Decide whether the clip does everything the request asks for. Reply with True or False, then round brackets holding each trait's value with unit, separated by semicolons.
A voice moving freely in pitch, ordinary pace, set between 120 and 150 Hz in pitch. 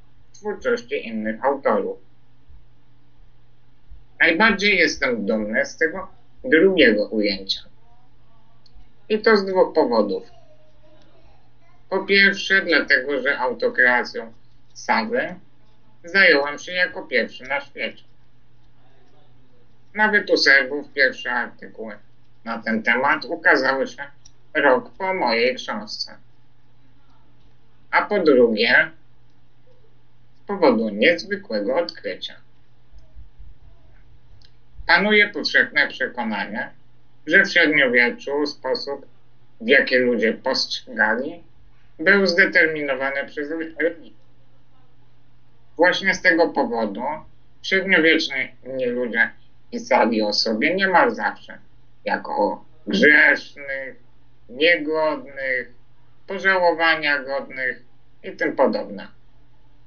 False (7.0 semitones; 80 wpm; 140 Hz)